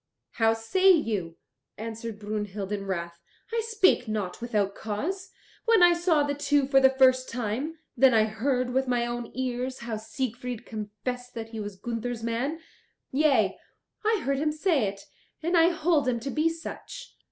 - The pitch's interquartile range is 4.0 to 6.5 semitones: Yes, average, 5.3 semitones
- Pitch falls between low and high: No, very high, 250 Hz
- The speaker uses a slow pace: No, average, 170 wpm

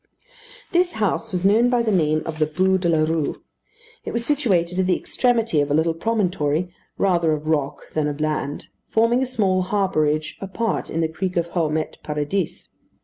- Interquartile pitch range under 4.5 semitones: No, average, 5.1 semitones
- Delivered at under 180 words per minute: No, average, 185 wpm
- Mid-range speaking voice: Yes, medium, 175 Hz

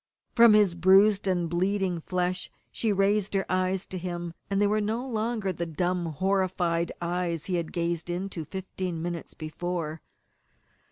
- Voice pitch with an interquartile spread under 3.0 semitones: Yes, narrow, 2.4 semitones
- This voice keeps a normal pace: Yes, average, 155 wpm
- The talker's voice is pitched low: No, medium, 185 Hz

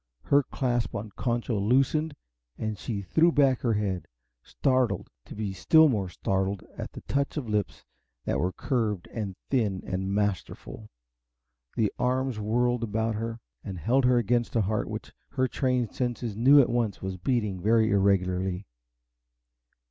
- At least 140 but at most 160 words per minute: Yes, average, 155 wpm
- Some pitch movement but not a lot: Yes, average, 4.0 semitones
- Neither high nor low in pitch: No, low, 110 Hz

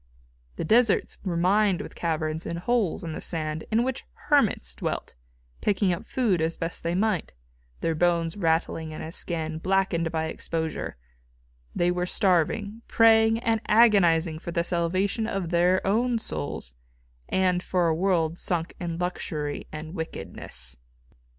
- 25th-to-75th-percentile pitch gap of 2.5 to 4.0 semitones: Yes, average, 3.5 semitones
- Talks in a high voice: No, medium, 175 Hz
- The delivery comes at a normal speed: Yes, average, 150 wpm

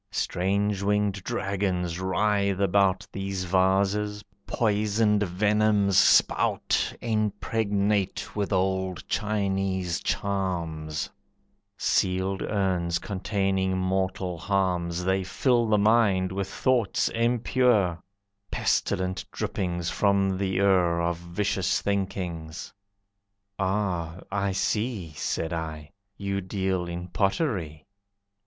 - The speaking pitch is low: Yes, very low, 95 Hz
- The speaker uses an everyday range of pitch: No, narrow, 2.1 semitones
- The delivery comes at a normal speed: No, slow, 95 wpm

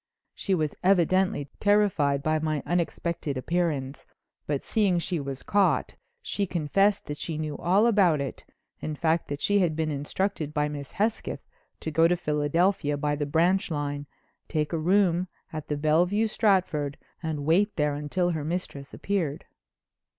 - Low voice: No, medium, 160 Hz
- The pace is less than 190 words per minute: Yes, average, 160 wpm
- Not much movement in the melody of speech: No, average, 4.0 semitones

